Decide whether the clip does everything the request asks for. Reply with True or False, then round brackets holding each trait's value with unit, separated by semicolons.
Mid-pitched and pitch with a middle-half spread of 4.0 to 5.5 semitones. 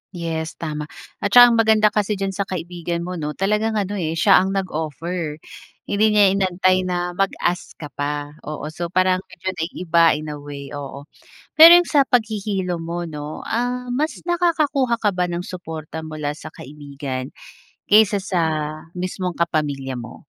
True (180 Hz; 4.7 semitones)